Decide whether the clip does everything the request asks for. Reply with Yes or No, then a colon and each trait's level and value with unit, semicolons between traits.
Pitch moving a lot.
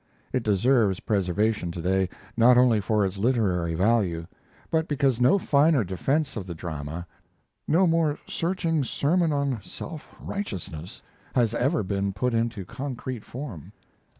Yes: wide, 6.8 semitones